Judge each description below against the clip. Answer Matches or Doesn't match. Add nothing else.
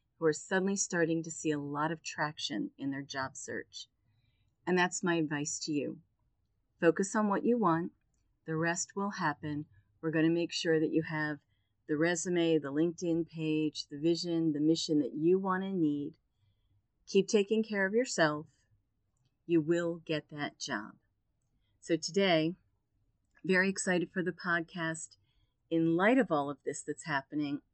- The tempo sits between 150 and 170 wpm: Matches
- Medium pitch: Matches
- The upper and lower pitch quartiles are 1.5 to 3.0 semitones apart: Doesn't match